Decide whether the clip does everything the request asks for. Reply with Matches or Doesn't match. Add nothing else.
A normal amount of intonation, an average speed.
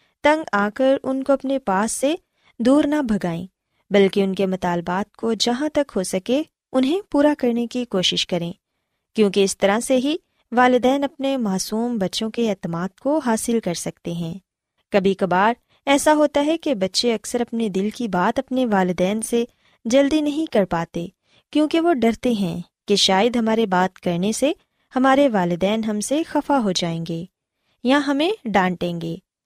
Doesn't match